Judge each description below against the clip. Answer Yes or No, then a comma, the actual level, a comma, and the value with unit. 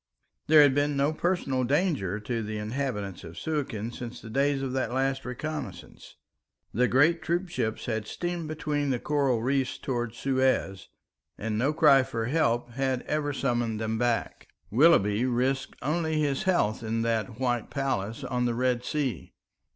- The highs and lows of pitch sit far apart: No, average, 3.9 semitones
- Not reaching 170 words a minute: Yes, average, 160 wpm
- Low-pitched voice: Yes, low, 130 Hz